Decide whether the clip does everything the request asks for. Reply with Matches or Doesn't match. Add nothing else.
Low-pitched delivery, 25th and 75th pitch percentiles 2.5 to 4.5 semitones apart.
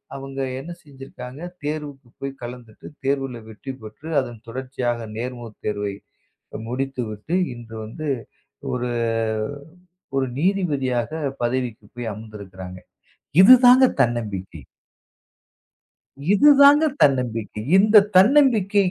Doesn't match